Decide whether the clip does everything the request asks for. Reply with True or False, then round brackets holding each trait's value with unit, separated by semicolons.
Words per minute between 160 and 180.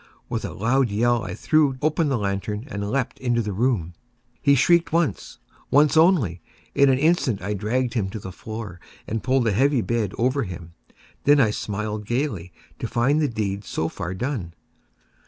True (175 wpm)